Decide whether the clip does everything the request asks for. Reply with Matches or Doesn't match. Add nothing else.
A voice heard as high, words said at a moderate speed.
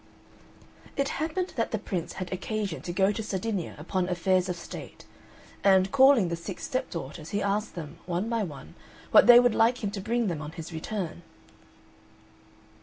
Matches